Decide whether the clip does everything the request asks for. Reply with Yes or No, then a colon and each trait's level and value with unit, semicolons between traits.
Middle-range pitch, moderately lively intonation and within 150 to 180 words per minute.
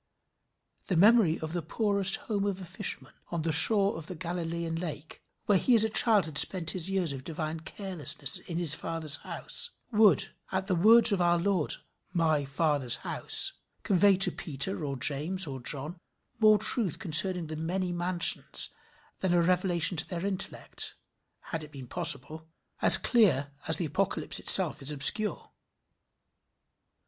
Yes: medium, 175 Hz; average, 3.7 semitones; average, 160 wpm